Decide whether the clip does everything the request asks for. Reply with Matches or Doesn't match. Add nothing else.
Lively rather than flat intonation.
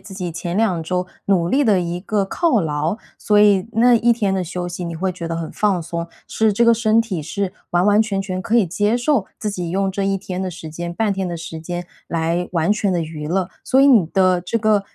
Doesn't match